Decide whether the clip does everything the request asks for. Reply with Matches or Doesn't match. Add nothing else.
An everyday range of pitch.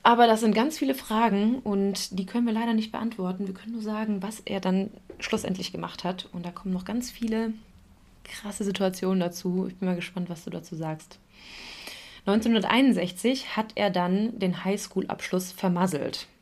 Matches